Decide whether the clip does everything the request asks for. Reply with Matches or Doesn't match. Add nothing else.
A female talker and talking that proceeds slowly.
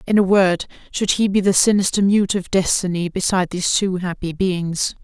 Doesn't match